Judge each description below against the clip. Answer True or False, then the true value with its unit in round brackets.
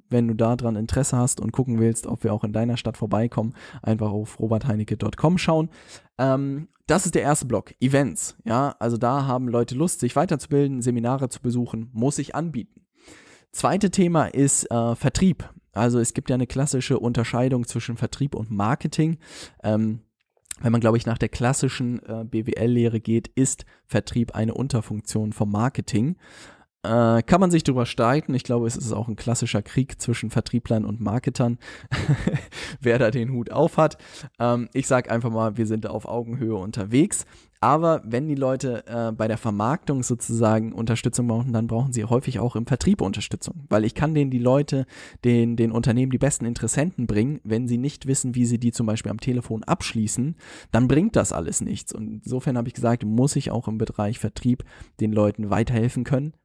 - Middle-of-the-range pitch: False (120 Hz)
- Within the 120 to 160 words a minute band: False (180 wpm)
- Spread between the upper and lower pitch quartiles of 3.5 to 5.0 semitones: False (3.1 semitones)